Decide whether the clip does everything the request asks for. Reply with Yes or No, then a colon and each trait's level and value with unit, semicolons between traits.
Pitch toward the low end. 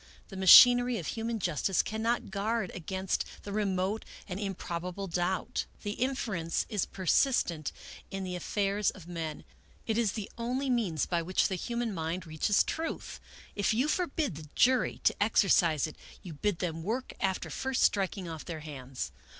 No: high, 195 Hz